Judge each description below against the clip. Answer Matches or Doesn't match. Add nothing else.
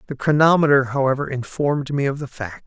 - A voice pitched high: Doesn't match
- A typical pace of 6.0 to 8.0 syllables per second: Matches